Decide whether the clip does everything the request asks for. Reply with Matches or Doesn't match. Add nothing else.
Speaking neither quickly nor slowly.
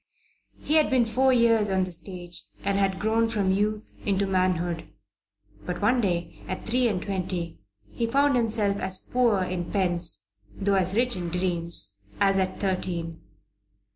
Matches